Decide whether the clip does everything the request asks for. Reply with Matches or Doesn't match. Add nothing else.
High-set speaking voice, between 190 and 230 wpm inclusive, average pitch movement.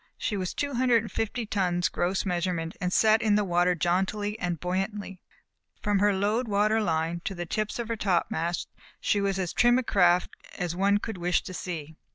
Matches